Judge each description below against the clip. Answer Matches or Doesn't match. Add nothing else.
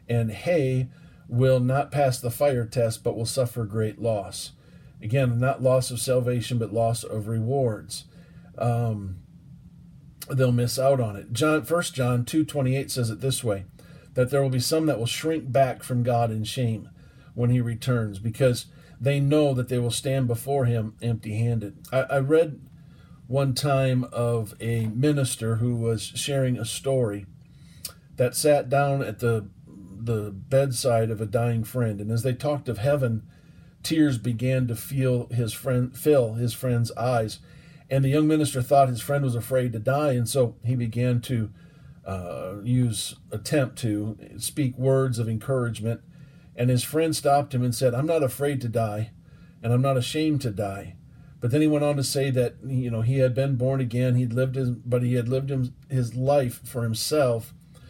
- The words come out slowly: Doesn't match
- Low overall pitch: Matches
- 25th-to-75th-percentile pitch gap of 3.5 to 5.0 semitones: Doesn't match